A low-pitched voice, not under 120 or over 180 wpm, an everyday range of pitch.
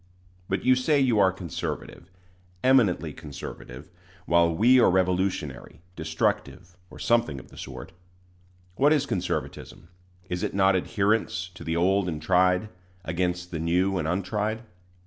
Yes: very low, 90 Hz; average, 140 wpm; average, 3.8 semitones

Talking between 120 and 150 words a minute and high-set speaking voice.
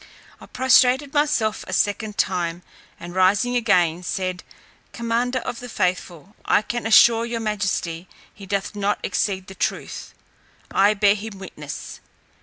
Yes: average, 140 wpm; high, 205 Hz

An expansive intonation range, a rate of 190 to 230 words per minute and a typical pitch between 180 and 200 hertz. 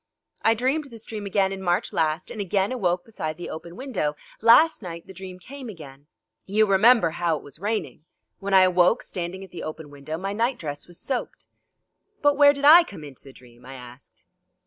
Yes: wide, 6.1 semitones; fast, 205 wpm; high, 190 Hz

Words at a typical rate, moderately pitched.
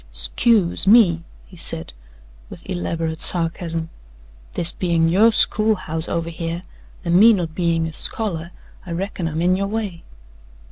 Yes: average, 145 wpm; medium, 170 Hz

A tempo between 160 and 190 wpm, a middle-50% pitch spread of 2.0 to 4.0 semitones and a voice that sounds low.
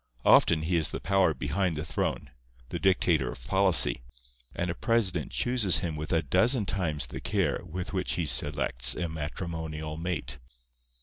Yes: average, 165 wpm; average, 3.4 semitones; very low, 85 Hz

